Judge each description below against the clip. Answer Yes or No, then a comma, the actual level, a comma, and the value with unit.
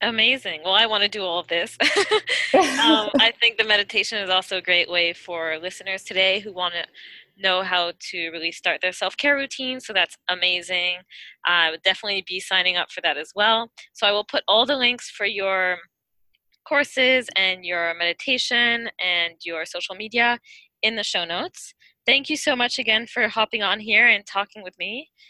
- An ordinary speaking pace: Yes, average, 195 wpm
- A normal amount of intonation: Yes, average, 4.9 semitones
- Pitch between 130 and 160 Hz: No, high, 205 Hz